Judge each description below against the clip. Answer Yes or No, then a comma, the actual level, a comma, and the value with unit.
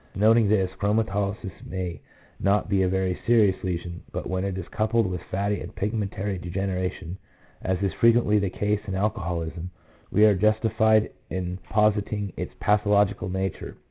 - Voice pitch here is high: No, low, 100 Hz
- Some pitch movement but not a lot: No, narrow, 2.2 semitones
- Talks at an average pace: Yes, average, 155 wpm